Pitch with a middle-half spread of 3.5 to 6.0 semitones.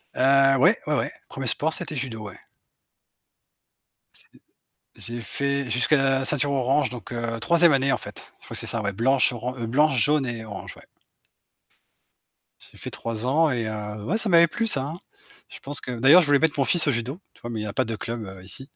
Yes: average, 4.0 semitones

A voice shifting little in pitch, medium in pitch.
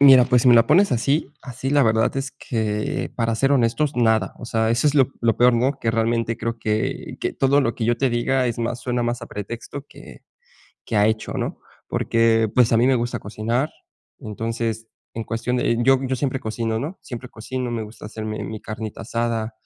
No: narrow, 2.3 semitones; low, 115 Hz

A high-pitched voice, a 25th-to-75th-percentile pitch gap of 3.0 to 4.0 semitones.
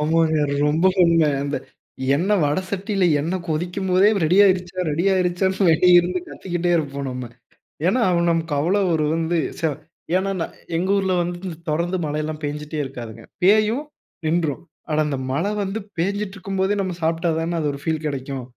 No: medium, 170 Hz; average, 3.7 semitones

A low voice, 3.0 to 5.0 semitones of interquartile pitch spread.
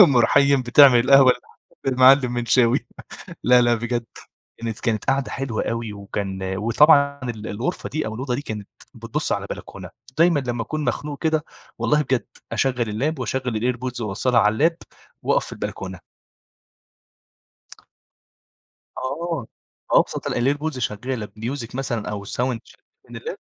Yes: low, 125 Hz; average, 3.5 semitones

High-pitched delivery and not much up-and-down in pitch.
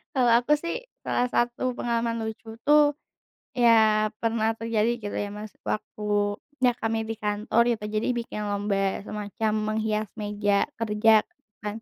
Yes: high, 220 Hz; narrow, 2.0 semitones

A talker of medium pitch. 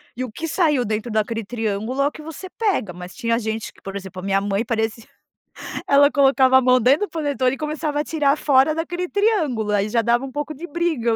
No: very high, 260 Hz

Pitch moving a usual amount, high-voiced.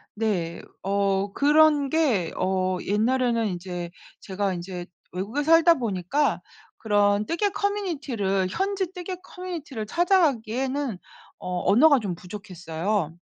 No: wide, 8.0 semitones; high, 215 Hz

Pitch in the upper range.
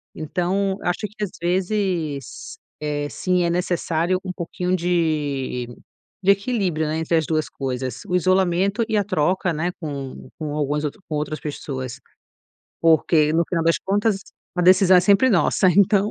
No: medium, 175 Hz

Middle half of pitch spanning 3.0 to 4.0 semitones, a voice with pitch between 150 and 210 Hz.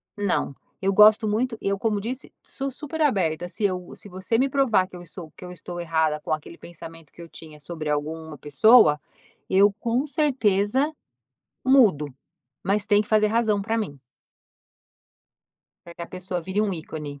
No: wide, 5.4 semitones; high, 195 Hz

